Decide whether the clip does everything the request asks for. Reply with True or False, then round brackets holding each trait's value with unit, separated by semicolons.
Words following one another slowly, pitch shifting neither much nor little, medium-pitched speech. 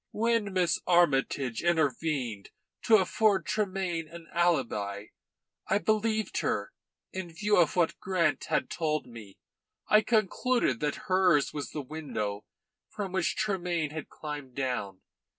False (130 wpm; 5.7 semitones; 170 Hz)